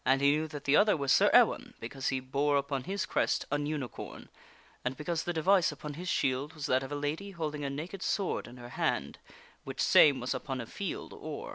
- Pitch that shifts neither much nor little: Yes, average, 3.2 semitones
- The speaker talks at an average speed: No, fast, 225 wpm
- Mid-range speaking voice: Yes, medium, 145 Hz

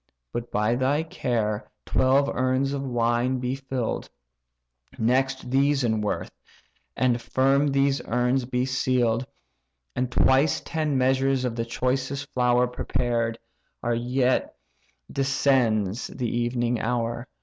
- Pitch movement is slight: Yes, narrow, 2.0 semitones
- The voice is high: No, low, 125 Hz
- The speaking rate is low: Yes, slow, 120 wpm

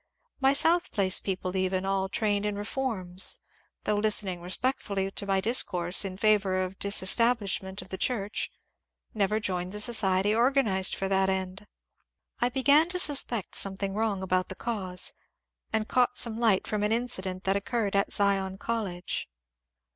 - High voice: Yes, high, 200 Hz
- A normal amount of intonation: Yes, average, 3.0 semitones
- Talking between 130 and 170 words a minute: Yes, average, 155 wpm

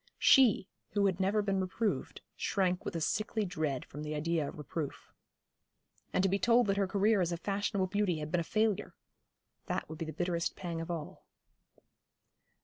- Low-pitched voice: No, medium, 185 Hz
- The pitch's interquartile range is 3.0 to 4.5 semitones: Yes, average, 3.7 semitones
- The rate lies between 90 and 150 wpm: No, average, 185 wpm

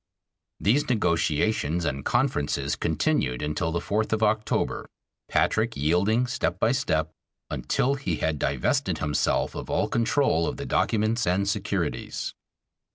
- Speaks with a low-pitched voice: Yes, very low, 95 Hz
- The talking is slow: Yes, slow, 130 wpm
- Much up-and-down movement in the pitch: Yes, wide, 5.9 semitones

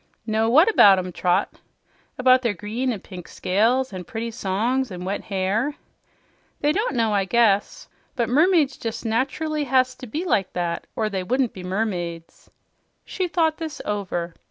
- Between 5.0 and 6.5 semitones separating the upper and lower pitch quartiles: Yes, wide, 5.5 semitones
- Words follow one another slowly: No, average, 165 wpm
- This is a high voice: Yes, high, 225 Hz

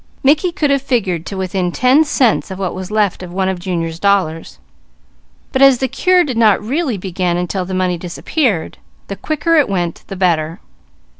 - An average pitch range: No, wide, 6.8 semitones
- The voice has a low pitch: No, high, 195 Hz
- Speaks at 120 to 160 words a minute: No, average, 190 wpm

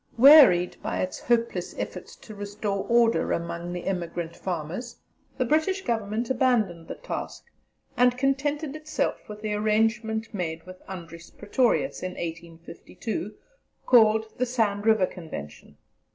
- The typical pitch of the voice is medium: No, high, 215 Hz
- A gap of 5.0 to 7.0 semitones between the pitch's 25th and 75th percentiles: Yes, average, 5.3 semitones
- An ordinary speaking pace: No, slow, 130 wpm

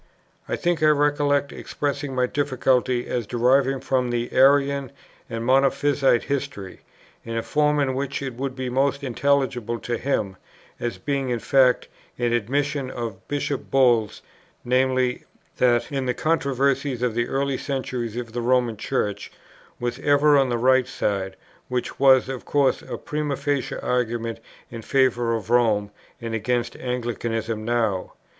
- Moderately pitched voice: No, low, 130 Hz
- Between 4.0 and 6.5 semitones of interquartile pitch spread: No, average, 2.7 semitones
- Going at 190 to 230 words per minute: No, average, 150 wpm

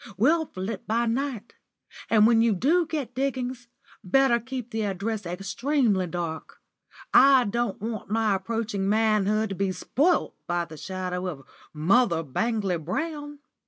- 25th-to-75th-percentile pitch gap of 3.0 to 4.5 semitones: No, average, 4.9 semitones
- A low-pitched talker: No, high, 220 Hz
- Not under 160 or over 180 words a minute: No, average, 140 wpm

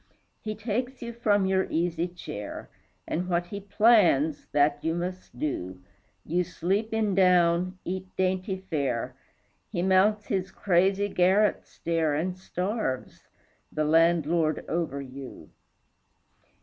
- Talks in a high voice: No, medium, 180 Hz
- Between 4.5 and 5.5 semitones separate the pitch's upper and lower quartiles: No, average, 3.3 semitones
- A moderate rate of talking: No, slow, 125 wpm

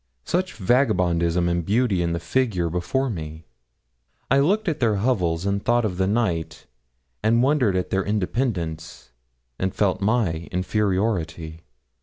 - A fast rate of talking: No, average, 140 wpm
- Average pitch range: No, wide, 5.7 semitones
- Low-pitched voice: Yes, very low, 95 Hz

